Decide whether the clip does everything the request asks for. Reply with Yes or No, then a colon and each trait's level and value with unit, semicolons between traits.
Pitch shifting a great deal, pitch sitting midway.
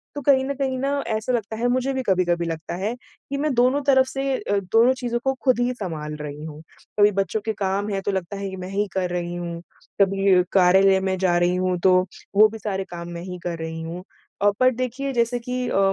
No: wide, 5.7 semitones; high, 200 Hz